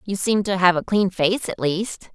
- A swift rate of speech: Yes, fast, 250 wpm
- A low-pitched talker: No, high, 190 Hz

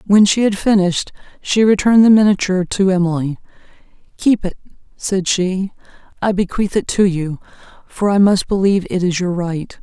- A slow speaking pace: No, average, 165 wpm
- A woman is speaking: Yes, female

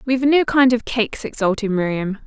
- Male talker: No, female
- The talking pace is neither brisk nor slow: No, fast, 210 wpm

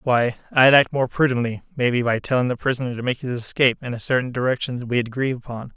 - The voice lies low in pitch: Yes, low, 125 Hz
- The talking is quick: Yes, fast, 230 wpm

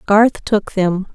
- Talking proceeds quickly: No, average, 160 wpm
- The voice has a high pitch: Yes, high, 200 Hz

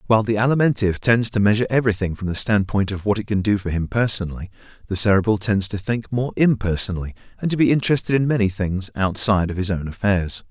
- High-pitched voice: No, low, 105 Hz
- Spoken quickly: Yes, fast, 210 wpm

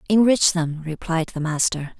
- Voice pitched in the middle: Yes, medium, 170 Hz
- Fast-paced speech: No, average, 150 wpm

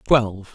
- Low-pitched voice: Yes, low, 110 Hz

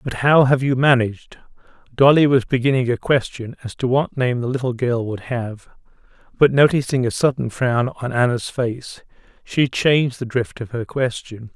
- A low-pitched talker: Yes, low, 125 Hz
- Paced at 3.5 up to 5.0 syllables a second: Yes, 4.8 syllables/s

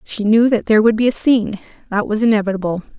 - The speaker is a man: No, female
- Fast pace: Yes, fast, 220 wpm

